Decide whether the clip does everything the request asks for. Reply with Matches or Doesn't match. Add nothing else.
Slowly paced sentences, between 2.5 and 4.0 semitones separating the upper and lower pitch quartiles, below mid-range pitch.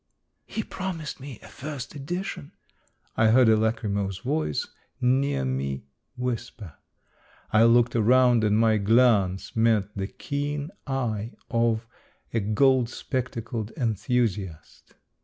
Matches